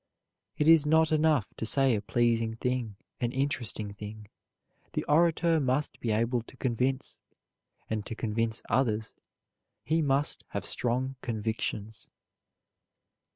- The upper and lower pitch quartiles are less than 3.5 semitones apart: No, average, 4.3 semitones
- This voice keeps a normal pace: No, slow, 125 wpm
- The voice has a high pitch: No, low, 125 Hz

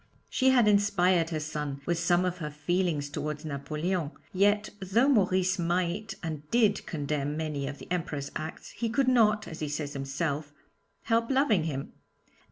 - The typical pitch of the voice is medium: Yes, medium, 170 Hz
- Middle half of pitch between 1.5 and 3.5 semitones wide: No, average, 5.3 semitones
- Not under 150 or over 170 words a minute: Yes, average, 165 wpm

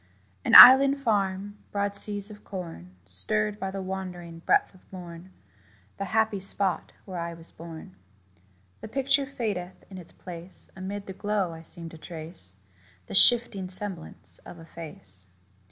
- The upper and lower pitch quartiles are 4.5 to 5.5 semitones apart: No, average, 3.5 semitones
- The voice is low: No, high, 190 Hz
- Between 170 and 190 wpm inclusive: No, average, 155 wpm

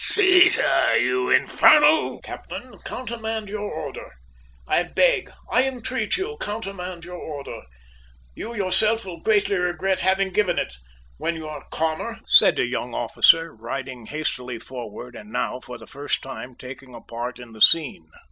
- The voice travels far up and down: Yes, wide, 8.6 semitones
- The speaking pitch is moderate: Yes, medium, 175 Hz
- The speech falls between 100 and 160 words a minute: Yes, average, 155 wpm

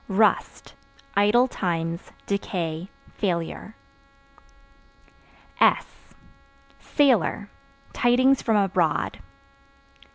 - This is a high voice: Yes, high, 200 Hz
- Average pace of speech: No, slow, 60 wpm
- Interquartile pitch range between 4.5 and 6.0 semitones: Yes, average, 5.2 semitones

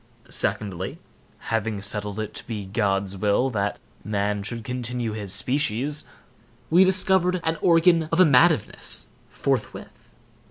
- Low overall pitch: Yes, low, 115 Hz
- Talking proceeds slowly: Yes, slow, 120 wpm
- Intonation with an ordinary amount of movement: No, wide, 7.2 semitones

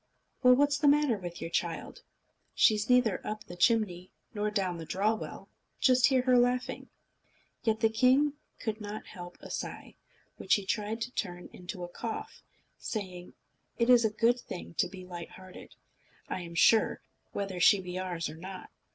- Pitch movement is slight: No, average, 5.1 semitones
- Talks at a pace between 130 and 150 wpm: No, average, 175 wpm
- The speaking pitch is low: No, high, 210 Hz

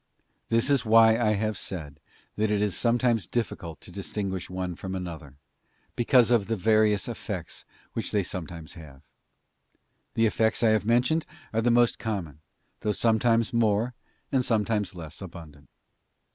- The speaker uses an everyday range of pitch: Yes, average, 4.1 semitones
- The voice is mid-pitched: No, low, 105 Hz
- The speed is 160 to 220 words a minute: No, average, 150 wpm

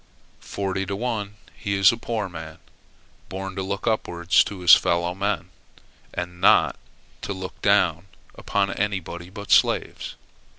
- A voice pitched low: Yes, very low, 95 Hz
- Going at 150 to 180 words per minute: No, average, 140 wpm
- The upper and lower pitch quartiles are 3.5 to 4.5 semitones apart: No, narrow, 2.4 semitones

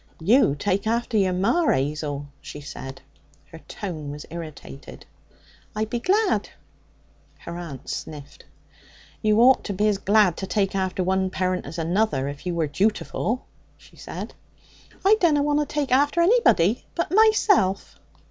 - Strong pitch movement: Yes, wide, 7.2 semitones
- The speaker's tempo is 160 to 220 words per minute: No, average, 150 wpm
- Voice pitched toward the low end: No, high, 195 Hz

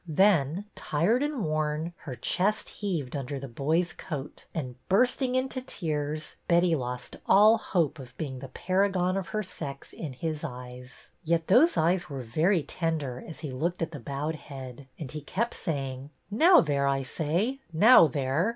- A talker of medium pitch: Yes, medium, 155 Hz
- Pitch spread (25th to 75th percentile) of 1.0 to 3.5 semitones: No, average, 5.3 semitones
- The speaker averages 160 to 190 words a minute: Yes, average, 170 wpm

